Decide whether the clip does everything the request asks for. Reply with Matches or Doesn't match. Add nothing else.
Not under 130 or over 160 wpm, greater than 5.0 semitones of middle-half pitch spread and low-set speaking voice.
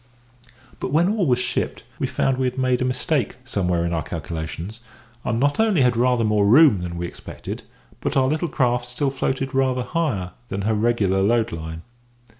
Doesn't match